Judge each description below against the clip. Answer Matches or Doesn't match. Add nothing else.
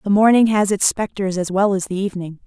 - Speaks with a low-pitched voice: Doesn't match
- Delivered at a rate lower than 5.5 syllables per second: Doesn't match